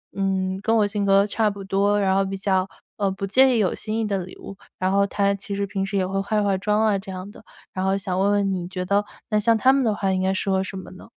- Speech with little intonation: Yes, narrow, 1.4 semitones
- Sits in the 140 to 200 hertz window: Yes, high, 195 Hz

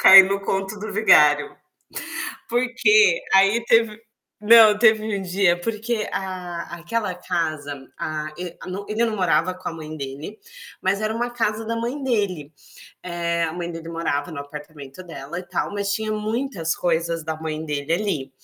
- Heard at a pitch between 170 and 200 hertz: Yes, medium, 185 Hz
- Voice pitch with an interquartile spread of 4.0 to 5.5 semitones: Yes, average, 4.8 semitones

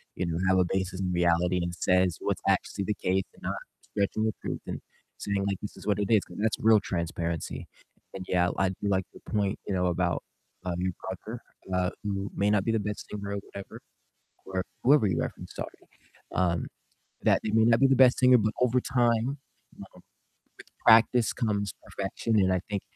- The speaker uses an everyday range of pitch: Yes, average, 3.0 semitones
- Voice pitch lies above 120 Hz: No, low, 100 Hz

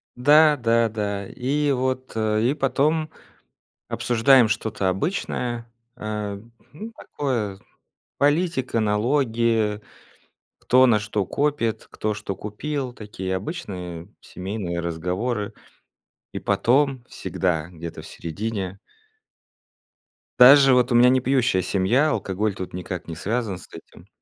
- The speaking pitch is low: Yes, low, 115 Hz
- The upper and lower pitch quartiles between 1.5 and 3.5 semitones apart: No, average, 4.8 semitones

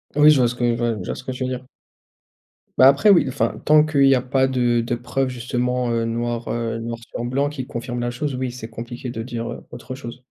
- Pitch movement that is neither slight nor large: No, narrow, 1.8 semitones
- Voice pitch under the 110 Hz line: No, low, 125 Hz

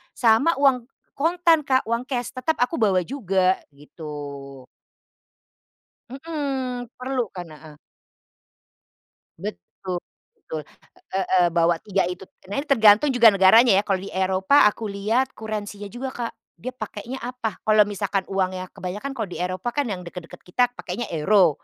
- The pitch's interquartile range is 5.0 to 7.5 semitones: Yes, wide, 5.4 semitones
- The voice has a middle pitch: No, high, 210 Hz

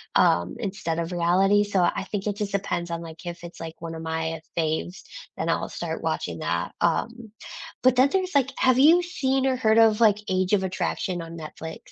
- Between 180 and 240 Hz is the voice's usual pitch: Yes, medium, 185 Hz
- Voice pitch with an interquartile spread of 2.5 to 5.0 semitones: No, wide, 5.5 semitones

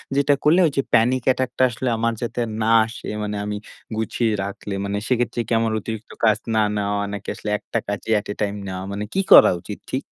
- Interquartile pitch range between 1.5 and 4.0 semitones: Yes, average, 2.9 semitones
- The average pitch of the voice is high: No, low, 110 Hz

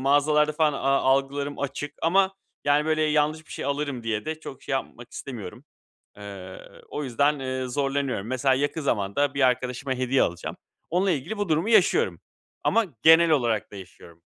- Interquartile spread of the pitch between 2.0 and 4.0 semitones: Yes, average, 3.3 semitones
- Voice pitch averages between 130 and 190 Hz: Yes, medium, 140 Hz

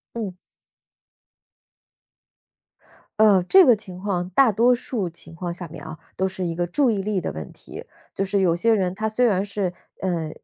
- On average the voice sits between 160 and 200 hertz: Yes, high, 190 Hz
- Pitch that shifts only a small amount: No, average, 3.6 semitones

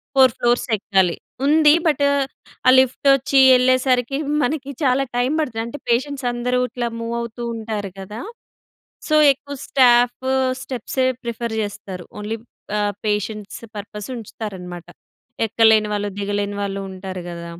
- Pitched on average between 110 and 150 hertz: No, high, 235 Hz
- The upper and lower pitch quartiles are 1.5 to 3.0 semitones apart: No, average, 3.9 semitones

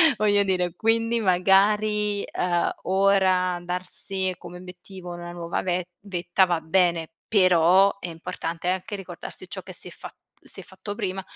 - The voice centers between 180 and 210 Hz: Yes, medium, 185 Hz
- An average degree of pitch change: No, narrow, 2.1 semitones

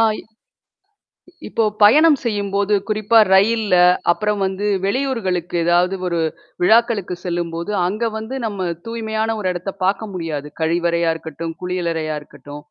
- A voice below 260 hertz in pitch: Yes, high, 190 Hz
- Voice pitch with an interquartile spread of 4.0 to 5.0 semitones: Yes, average, 4.3 semitones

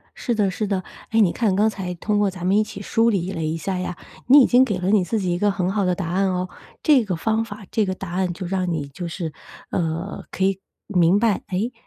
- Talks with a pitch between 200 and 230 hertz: No, high, 190 Hz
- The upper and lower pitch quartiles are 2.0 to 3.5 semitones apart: Yes, average, 2.8 semitones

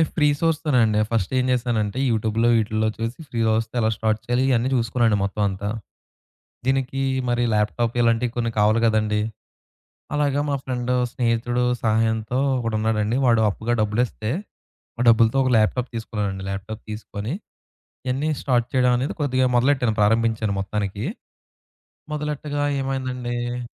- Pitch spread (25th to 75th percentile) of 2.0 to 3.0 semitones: Yes, narrow, 2.6 semitones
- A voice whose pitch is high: No, low, 115 Hz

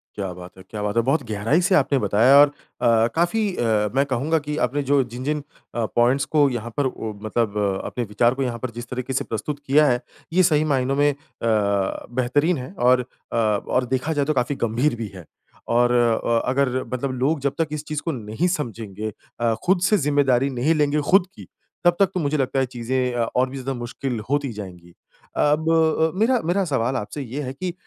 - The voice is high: No, low, 130 Hz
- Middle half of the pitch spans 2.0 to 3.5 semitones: No, average, 4.1 semitones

